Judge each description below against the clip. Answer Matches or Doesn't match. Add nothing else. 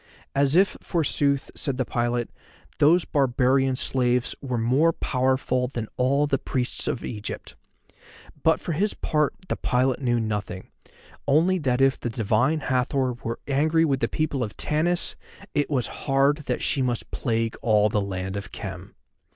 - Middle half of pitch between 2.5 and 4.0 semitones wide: Matches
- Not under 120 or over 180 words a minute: Matches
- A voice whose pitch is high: Doesn't match